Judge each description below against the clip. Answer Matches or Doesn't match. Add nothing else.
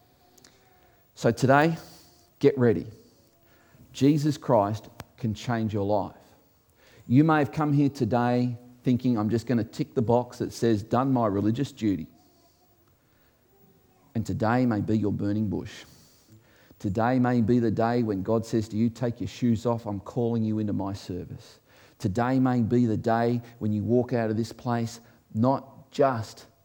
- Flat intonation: Matches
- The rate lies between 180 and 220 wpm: Doesn't match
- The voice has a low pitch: Matches